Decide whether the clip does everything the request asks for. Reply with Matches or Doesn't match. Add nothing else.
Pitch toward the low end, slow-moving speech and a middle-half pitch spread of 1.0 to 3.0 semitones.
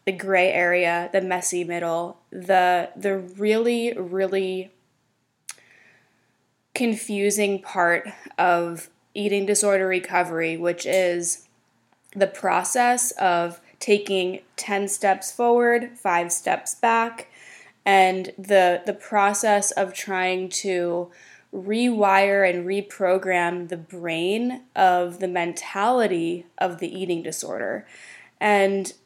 Doesn't match